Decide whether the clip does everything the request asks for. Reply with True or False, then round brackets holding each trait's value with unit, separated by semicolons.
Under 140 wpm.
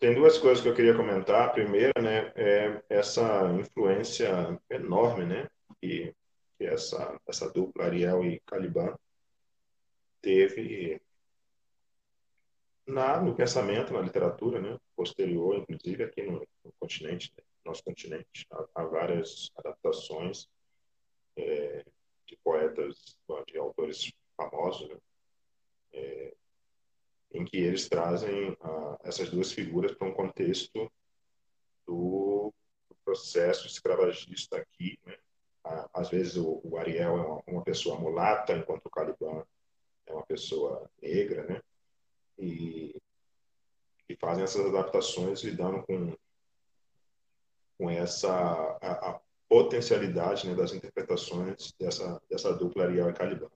True (120 wpm)